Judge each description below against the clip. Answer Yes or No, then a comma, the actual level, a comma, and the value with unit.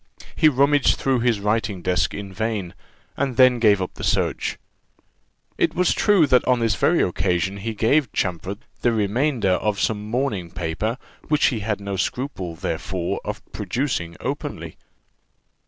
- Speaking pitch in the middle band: No, low, 110 Hz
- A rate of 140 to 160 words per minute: Yes, average, 155 wpm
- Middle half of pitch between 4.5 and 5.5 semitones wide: Yes, average, 5.0 semitones